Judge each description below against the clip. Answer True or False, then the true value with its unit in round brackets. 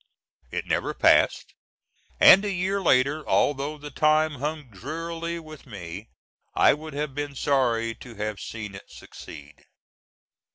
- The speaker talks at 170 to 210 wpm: False (135 wpm)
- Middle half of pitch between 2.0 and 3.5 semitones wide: False (5.3 semitones)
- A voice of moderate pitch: True (145 Hz)